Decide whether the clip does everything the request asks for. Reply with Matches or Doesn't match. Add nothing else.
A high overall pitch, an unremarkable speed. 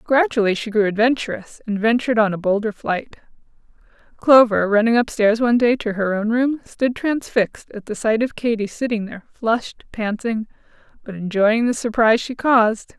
Matches